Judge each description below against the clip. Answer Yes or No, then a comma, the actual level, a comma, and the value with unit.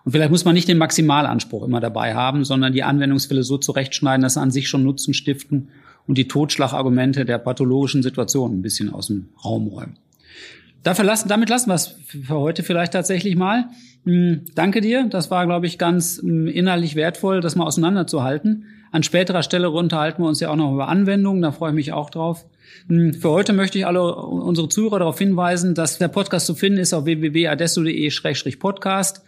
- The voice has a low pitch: No, medium, 165 Hz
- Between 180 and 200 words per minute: Yes, average, 185 wpm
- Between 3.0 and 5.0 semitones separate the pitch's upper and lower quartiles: Yes, average, 4.5 semitones